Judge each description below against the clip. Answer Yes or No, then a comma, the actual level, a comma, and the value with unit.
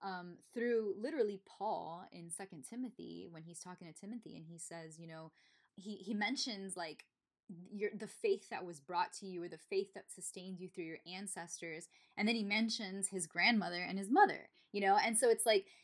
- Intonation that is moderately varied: Yes, average, 4.1 semitones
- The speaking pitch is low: No, high, 195 Hz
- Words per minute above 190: Yes, average, 200 wpm